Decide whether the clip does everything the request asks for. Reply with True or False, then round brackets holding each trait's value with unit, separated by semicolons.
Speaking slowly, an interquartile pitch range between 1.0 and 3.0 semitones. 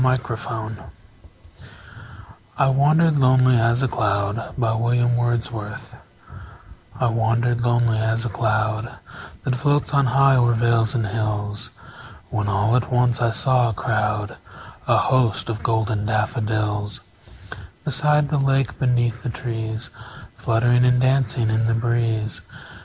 True (125 wpm; 2.4 semitones)